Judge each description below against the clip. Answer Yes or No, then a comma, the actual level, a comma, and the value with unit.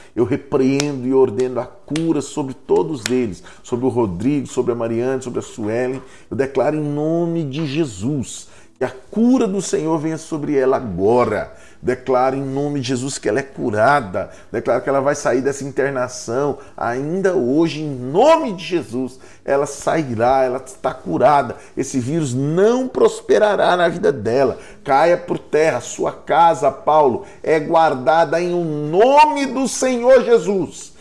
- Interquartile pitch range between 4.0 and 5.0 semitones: Yes, average, 4.5 semitones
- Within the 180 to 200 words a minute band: No, average, 155 wpm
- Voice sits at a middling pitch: Yes, medium, 145 Hz